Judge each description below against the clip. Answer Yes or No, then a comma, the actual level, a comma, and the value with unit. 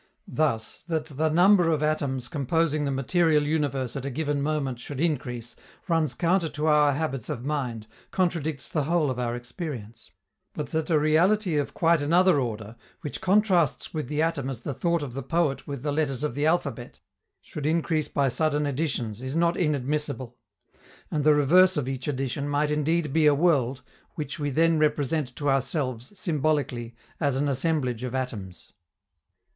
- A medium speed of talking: Yes, average, 175 wpm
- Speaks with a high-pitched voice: No, medium, 145 Hz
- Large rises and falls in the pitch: No, average, 3.4 semitones